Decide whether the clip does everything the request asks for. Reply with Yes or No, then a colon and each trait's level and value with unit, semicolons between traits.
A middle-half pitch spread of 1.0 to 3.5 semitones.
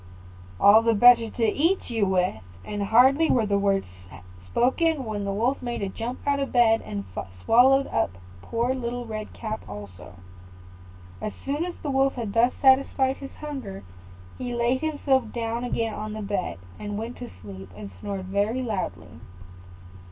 No: average, 4.4 semitones